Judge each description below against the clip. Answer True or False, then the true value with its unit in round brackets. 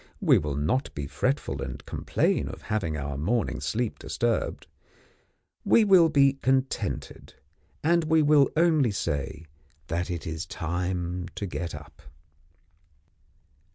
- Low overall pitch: True (100 Hz)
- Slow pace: True (120 wpm)